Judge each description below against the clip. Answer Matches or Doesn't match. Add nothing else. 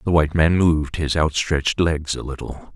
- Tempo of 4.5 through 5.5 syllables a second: Matches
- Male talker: Matches